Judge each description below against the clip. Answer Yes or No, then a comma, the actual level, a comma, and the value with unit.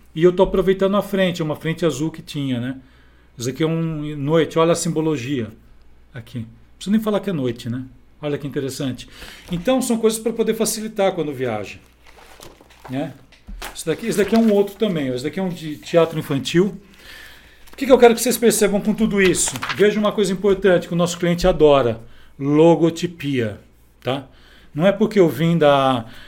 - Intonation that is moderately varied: No, wide, 6.8 semitones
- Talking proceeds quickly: Yes, fast, 190 wpm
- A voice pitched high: No, medium, 165 Hz